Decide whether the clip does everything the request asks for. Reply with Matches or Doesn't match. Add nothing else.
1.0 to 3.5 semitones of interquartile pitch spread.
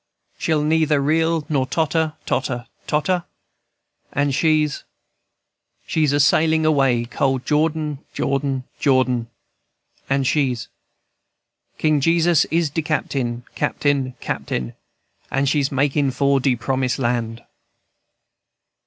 Matches